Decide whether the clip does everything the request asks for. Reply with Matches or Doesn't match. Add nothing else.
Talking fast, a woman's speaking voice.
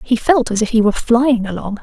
Matches